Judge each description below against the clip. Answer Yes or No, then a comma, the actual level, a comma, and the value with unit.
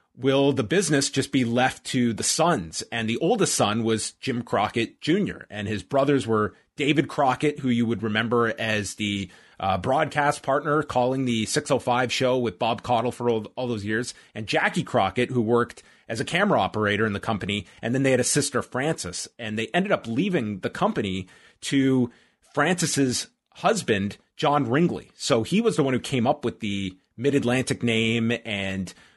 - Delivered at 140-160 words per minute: No, average, 185 wpm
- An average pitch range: Yes, average, 4.0 semitones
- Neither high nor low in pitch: No, low, 120 Hz